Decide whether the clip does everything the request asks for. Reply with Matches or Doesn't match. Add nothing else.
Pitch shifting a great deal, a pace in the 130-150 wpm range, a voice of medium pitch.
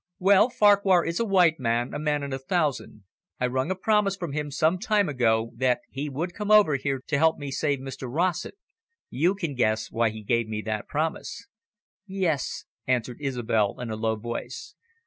Doesn't match